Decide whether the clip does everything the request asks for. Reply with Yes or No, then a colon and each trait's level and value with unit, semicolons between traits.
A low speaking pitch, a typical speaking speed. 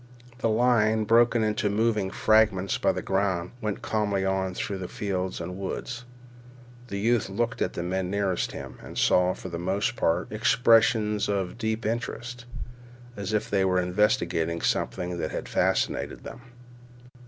Yes: low, 100 Hz; average, 155 wpm